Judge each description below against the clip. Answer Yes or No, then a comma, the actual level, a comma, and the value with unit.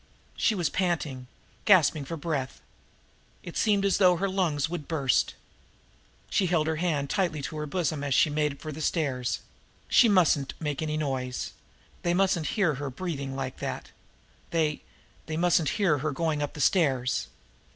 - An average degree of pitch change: Yes, average, 3.8 semitones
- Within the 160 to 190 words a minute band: Yes, average, 170 wpm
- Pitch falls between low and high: Yes, medium, 155 Hz